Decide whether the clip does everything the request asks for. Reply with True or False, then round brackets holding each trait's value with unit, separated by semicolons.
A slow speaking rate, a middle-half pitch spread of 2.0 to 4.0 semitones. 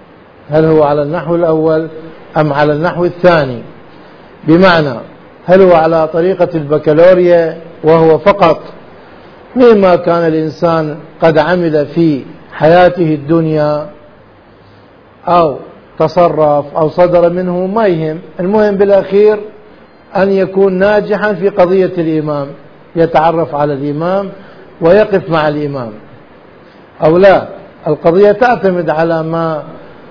False (105 wpm; 2.9 semitones)